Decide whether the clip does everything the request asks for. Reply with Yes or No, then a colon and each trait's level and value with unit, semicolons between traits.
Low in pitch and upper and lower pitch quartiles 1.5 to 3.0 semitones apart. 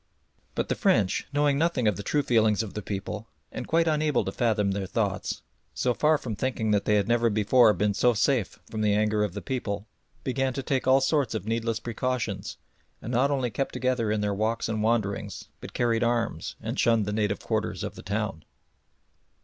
No: low, 115 Hz; average, 3.6 semitones